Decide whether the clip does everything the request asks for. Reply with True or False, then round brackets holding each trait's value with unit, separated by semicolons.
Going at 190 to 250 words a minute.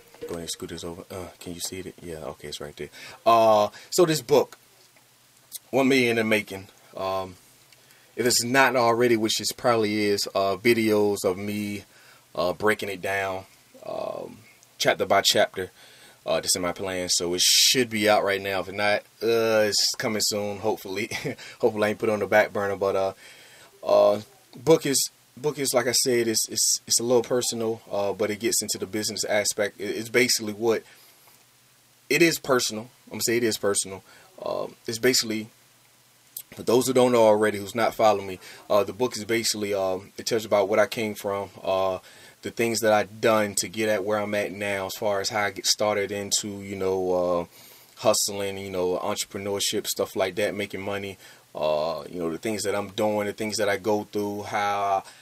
True (200 wpm)